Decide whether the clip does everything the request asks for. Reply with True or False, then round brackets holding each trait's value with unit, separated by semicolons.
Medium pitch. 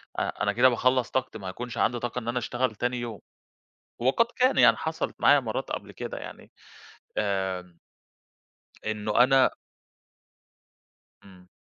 False (120 Hz)